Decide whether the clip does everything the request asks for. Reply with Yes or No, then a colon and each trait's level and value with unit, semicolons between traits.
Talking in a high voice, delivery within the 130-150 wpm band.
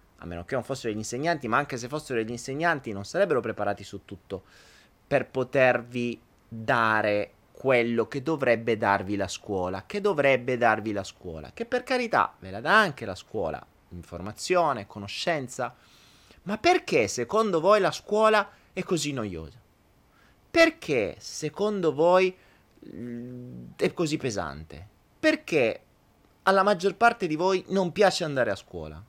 No: low, 125 Hz; average, 140 wpm